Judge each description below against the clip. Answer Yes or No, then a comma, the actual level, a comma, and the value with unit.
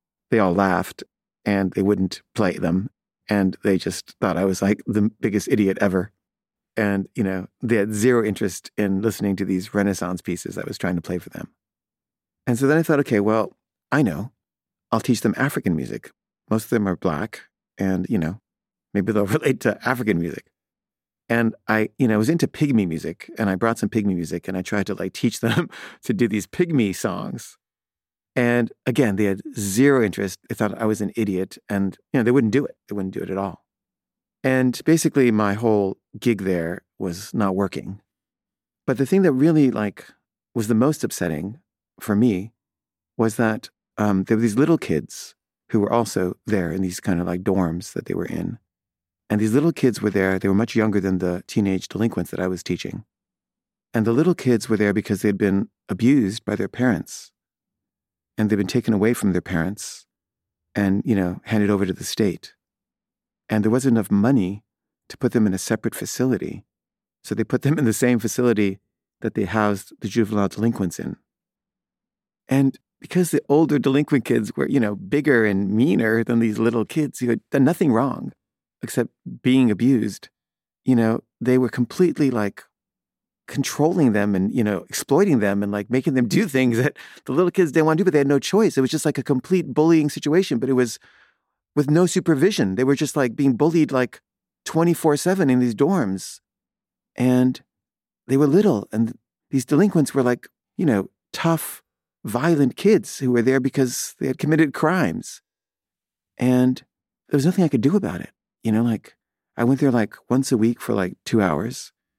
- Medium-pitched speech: No, low, 115 Hz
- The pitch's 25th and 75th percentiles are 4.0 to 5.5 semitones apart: Yes, average, 5.1 semitones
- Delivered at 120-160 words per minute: No, average, 195 wpm